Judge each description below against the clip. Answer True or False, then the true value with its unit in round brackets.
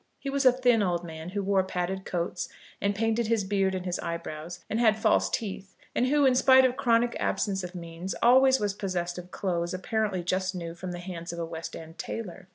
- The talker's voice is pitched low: False (190 Hz)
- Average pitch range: True (4.4 semitones)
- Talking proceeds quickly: True (220 wpm)